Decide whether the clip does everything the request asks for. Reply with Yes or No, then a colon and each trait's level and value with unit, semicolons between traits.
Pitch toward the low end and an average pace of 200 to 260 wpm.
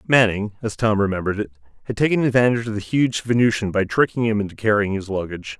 Yes: low, 110 Hz; fast, 205 wpm